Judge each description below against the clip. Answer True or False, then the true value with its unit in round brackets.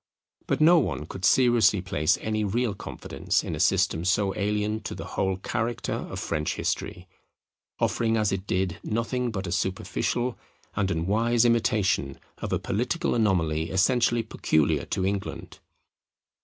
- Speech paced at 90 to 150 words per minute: True (145 wpm)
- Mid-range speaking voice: False (105 Hz)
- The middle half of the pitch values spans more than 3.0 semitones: True (3.8 semitones)